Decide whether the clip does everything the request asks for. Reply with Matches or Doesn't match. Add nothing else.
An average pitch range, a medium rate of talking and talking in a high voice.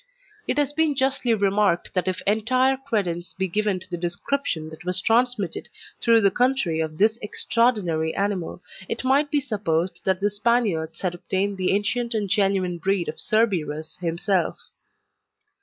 Matches